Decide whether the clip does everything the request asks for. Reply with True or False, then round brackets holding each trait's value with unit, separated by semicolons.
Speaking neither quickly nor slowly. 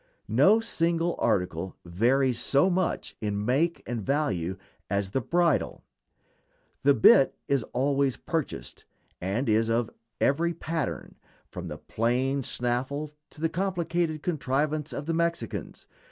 False (125 wpm)